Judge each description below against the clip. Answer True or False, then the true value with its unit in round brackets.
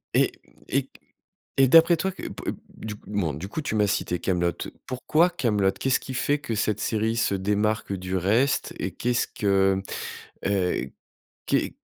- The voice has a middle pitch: False (105 Hz)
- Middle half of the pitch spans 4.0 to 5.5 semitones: True (5.0 semitones)